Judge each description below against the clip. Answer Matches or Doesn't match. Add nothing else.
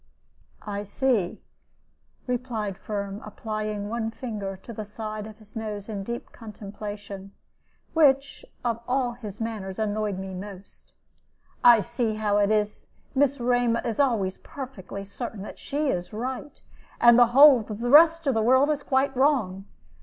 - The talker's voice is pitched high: Matches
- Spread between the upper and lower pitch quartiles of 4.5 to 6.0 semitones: Doesn't match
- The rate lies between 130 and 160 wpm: Matches